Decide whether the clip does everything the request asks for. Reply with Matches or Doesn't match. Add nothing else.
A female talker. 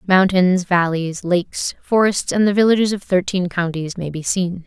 Matches